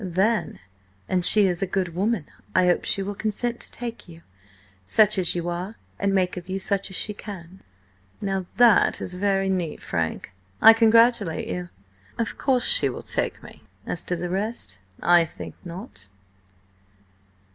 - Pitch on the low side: No, high, 190 Hz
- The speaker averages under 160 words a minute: No, average, 165 wpm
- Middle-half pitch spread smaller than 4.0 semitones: Yes, average, 3.5 semitones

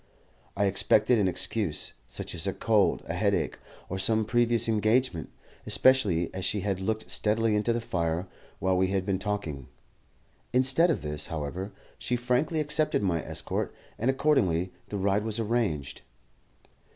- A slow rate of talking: No, average, 150 wpm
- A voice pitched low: Yes, low, 105 Hz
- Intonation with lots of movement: No, average, 4.3 semitones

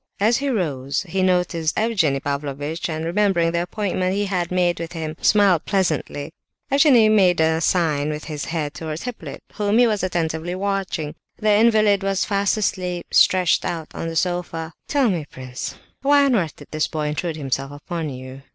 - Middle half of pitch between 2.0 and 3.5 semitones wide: No, average, 4.4 semitones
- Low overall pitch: No, medium, 175 Hz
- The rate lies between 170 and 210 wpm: Yes, average, 180 wpm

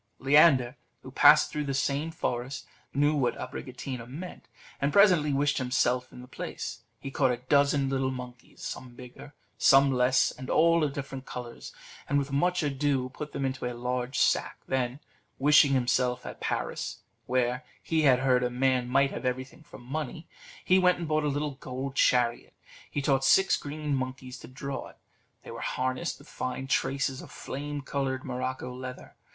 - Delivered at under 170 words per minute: No, average, 180 wpm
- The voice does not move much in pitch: Yes, narrow, 2.2 semitones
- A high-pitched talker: No, low, 135 Hz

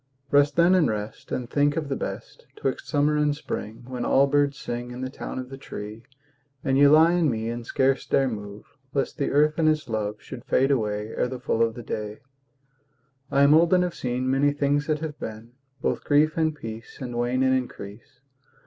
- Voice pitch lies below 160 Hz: Yes, low, 135 Hz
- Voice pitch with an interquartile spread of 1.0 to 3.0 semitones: No, average, 3.7 semitones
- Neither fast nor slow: No, fast, 210 wpm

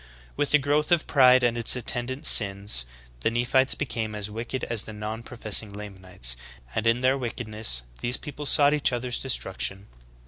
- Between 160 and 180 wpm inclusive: Yes, average, 175 wpm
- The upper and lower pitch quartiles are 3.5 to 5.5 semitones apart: Yes, average, 3.9 semitones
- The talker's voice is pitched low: Yes, low, 115 Hz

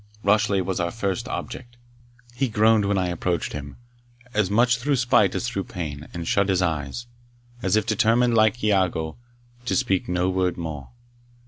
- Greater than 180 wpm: No, average, 165 wpm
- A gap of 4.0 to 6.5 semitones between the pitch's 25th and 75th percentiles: Yes, average, 4.5 semitones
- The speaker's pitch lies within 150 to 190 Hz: No, low, 100 Hz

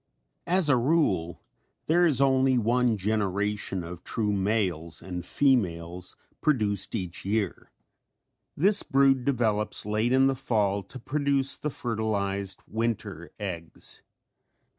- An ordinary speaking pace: No, slow, 120 wpm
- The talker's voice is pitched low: Yes, low, 110 Hz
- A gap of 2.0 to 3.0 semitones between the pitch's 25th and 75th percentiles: No, wide, 5.4 semitones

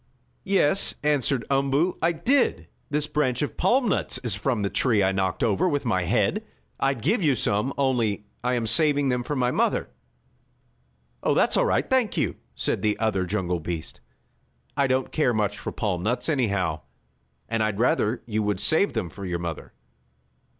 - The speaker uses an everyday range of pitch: No, wide, 5.9 semitones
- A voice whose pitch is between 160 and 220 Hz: No, low, 120 Hz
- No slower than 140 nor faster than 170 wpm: No, average, 180 wpm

